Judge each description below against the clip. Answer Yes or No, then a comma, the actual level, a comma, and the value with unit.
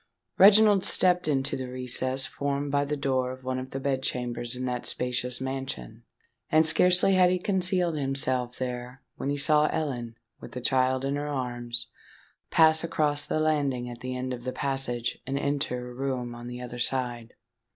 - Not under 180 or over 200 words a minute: Yes, average, 185 wpm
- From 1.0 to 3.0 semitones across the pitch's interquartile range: Yes, average, 2.7 semitones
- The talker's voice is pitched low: Yes, low, 130 Hz